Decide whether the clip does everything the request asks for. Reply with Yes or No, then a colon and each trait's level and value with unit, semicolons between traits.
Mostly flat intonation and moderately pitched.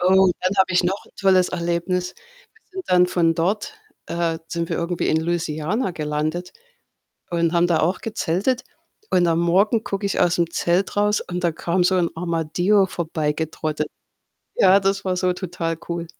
Yes: narrow, 2.2 semitones; medium, 175 Hz